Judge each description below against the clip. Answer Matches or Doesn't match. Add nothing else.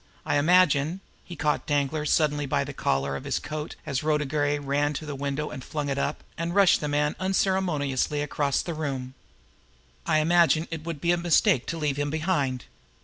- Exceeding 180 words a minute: Matches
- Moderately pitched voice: Matches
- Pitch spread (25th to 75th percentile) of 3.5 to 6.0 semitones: Doesn't match